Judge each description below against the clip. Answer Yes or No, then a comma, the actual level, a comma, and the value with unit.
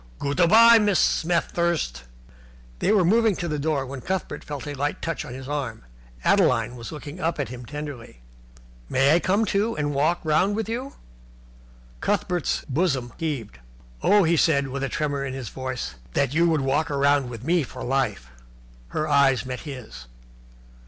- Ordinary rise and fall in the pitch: Yes, average, 4.6 semitones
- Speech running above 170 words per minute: Yes, average, 180 wpm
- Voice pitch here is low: No, medium, 145 Hz